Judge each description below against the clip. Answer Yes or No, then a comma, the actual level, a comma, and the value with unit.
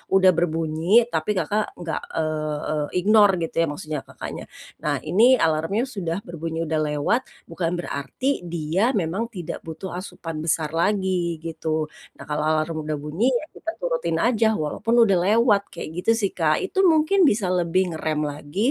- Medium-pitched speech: Yes, medium, 170 Hz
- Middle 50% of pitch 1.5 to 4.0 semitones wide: No, average, 4.6 semitones